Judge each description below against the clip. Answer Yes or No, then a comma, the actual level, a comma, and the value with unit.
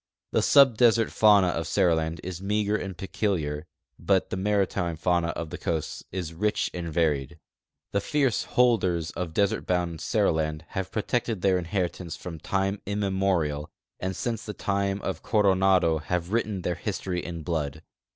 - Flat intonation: No, average, 3.5 semitones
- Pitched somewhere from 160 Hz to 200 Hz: No, very low, 90 Hz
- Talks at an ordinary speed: Yes, average, 150 wpm